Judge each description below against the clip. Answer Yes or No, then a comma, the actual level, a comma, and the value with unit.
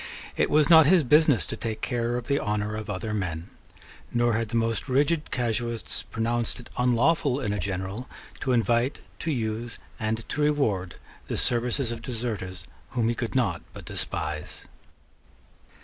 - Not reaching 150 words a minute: No, average, 165 wpm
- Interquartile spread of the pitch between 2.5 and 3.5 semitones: Yes, average, 3.1 semitones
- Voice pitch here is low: Yes, low, 115 Hz